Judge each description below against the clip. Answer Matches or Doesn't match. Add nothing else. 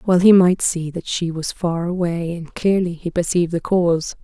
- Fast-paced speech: Matches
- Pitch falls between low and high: Matches